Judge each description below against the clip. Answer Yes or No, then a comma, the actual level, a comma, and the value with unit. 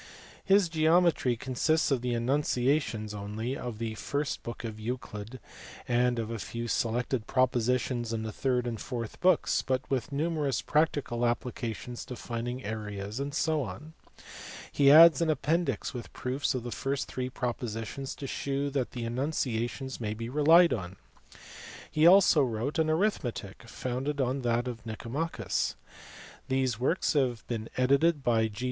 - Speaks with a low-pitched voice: Yes, low, 125 Hz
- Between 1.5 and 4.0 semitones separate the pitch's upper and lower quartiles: Yes, average, 3.7 semitones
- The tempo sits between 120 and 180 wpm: Yes, average, 150 wpm